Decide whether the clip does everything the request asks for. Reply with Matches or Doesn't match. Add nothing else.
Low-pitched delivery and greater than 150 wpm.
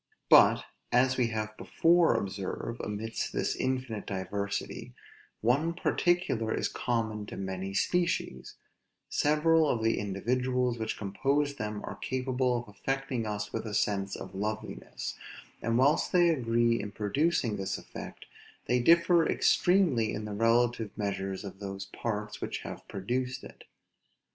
Doesn't match